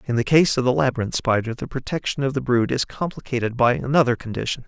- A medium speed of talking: No, fast, 220 wpm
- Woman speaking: No, male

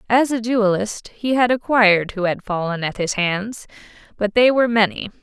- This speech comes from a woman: Yes, female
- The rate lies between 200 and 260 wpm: No, average, 185 wpm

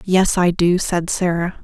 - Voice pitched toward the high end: No, medium, 175 Hz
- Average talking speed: Yes, average, 185 wpm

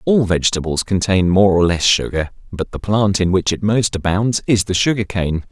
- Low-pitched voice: Yes, very low, 95 Hz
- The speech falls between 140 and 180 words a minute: No, fast, 205 wpm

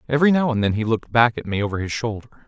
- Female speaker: No, male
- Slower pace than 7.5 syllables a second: No, 8.0 syllables/s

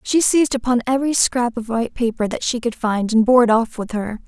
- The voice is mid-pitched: No, high, 235 Hz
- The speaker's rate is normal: No, fast, 255 wpm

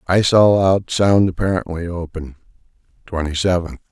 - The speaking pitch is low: Yes, very low, 90 Hz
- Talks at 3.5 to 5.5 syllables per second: Yes, 5.1 syllables/s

